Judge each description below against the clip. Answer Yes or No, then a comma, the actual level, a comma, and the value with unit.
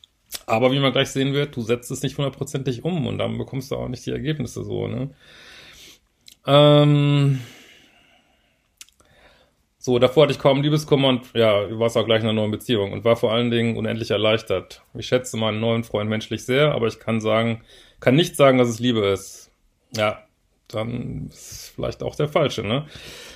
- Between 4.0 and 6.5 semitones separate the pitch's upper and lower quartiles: No, average, 3.4 semitones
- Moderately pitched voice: No, low, 125 Hz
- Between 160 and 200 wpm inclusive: Yes, fast, 190 wpm